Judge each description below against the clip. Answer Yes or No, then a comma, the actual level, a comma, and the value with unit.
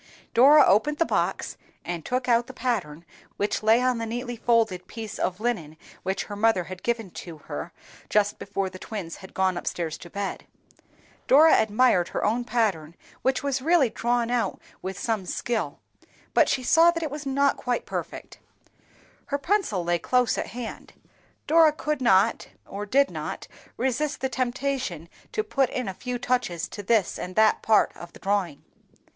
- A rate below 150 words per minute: No, average, 175 wpm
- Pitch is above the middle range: Yes, high, 230 Hz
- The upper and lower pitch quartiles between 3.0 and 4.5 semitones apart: No, average, 5.3 semitones